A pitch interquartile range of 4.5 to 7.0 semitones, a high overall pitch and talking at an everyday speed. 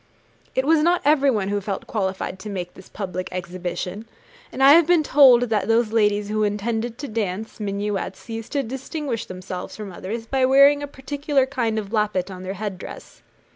Yes: average, 5.2 semitones; high, 220 Hz; average, 185 wpm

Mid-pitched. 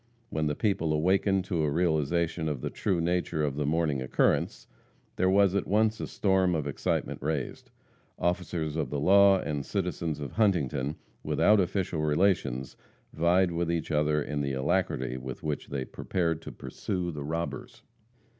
No: very low, 80 Hz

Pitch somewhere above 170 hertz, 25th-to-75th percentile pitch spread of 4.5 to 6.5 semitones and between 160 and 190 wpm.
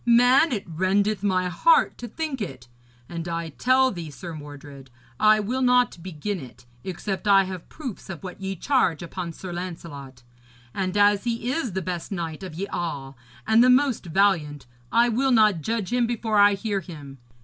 Yes: high, 190 Hz; wide, 5.5 semitones; average, 180 wpm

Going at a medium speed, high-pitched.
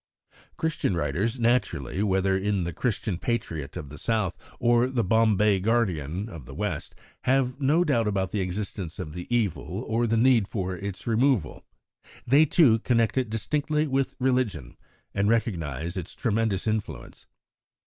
No: average, 150 wpm; low, 110 Hz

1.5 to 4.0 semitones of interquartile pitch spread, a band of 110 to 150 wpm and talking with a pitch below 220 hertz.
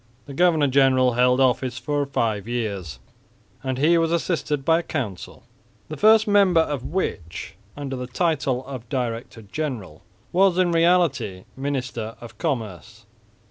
No: wide, 5.5 semitones; average, 140 wpm; low, 135 Hz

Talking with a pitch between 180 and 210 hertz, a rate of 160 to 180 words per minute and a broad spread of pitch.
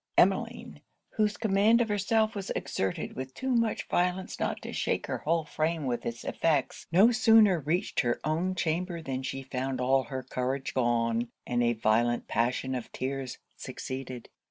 No: medium, 140 Hz; average, 165 wpm; wide, 6.9 semitones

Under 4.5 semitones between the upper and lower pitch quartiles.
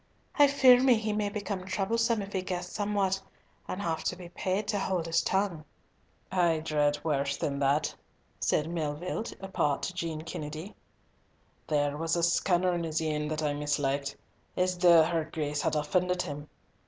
Yes: average, 4.1 semitones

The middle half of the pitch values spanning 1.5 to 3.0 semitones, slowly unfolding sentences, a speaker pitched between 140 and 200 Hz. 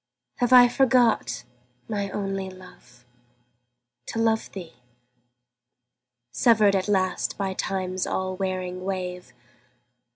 Yes: narrow, 2.6 semitones; slow, 100 wpm; high, 190 Hz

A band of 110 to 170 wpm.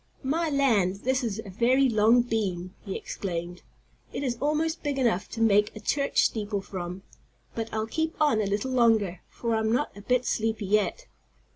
No: average, 180 wpm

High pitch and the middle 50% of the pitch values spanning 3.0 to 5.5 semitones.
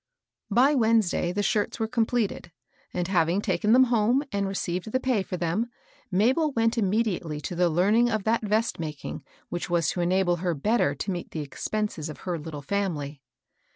Yes: high, 195 Hz; average, 4.6 semitones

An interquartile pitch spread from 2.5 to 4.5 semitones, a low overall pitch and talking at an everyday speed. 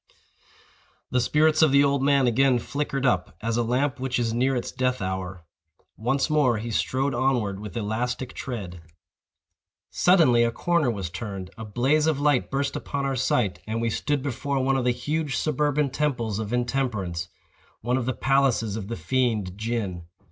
Yes: average, 3.8 semitones; low, 125 Hz; average, 170 wpm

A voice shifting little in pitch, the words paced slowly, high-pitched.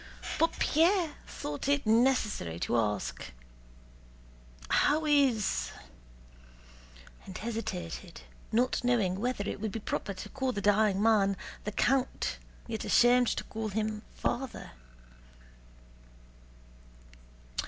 No: average, 4.3 semitones; slow, 105 wpm; high, 220 Hz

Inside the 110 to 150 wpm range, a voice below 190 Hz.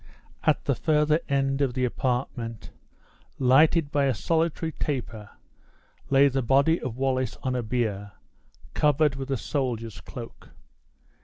Yes: slow, 135 wpm; low, 135 Hz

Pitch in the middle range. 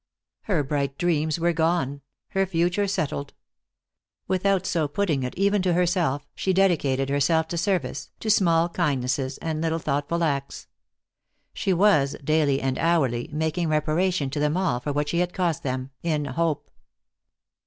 Yes: medium, 160 Hz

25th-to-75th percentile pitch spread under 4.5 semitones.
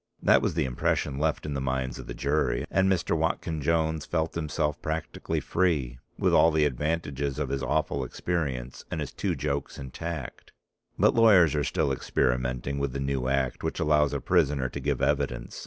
Yes: average, 3.2 semitones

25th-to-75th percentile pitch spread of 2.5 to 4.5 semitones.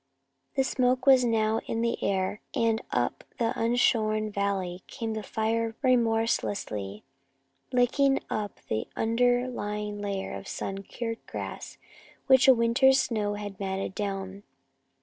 Yes: average, 3.4 semitones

